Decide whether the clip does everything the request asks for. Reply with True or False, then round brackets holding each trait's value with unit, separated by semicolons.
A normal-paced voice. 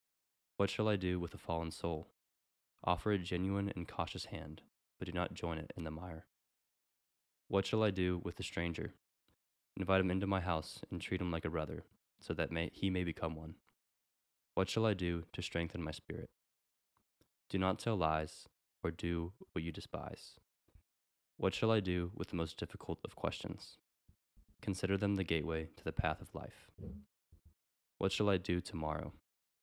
True (180 wpm)